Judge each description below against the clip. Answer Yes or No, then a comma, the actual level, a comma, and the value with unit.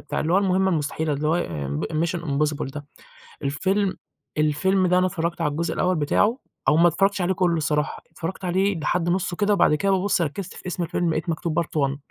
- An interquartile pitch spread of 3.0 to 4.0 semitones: Yes, average, 3.5 semitones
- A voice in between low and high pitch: Yes, medium, 170 Hz